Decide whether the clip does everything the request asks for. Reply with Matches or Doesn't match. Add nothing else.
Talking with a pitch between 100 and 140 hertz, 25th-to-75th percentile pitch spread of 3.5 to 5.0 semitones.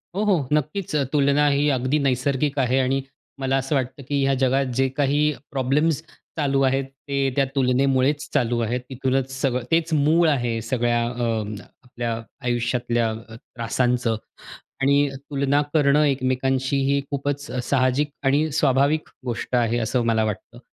Doesn't match